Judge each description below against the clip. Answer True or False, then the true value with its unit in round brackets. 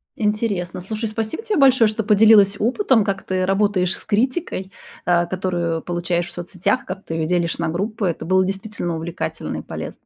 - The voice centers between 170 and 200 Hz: True (190 Hz)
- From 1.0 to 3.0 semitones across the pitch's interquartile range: False (3.6 semitones)